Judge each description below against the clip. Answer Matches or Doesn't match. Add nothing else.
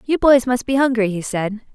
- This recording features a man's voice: Doesn't match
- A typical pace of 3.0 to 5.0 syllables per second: Doesn't match